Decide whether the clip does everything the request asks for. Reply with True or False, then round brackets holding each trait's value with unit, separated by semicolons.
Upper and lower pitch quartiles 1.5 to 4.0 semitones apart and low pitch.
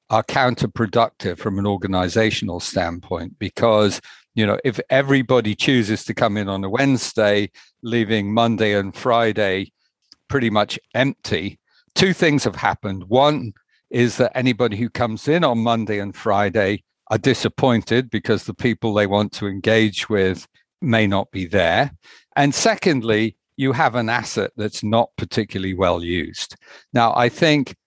True (3.3 semitones; 110 Hz)